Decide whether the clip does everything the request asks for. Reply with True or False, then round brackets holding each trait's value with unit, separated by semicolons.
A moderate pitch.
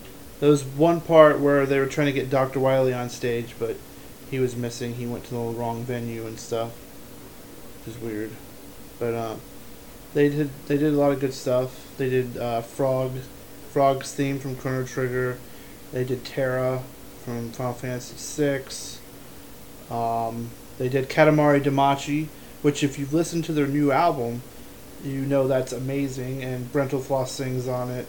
False (130 Hz)